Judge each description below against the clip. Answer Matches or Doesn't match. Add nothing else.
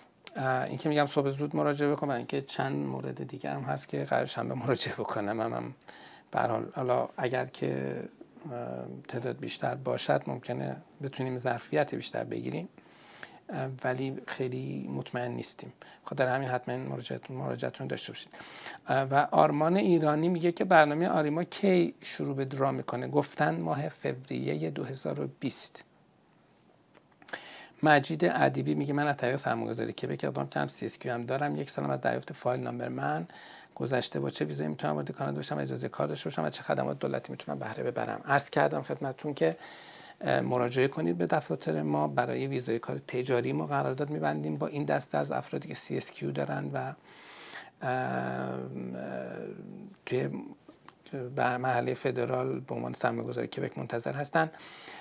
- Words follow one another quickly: Doesn't match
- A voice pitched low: Matches